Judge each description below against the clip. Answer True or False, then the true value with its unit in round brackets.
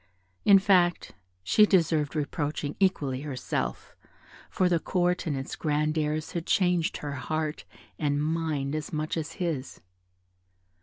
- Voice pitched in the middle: True (155 Hz)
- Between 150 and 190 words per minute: False (135 wpm)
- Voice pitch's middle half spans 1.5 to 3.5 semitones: True (3.1 semitones)